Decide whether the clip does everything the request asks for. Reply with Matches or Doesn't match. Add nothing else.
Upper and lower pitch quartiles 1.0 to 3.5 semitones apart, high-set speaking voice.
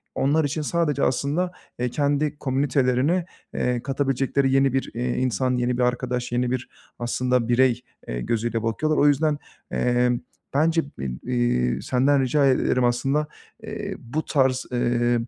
Doesn't match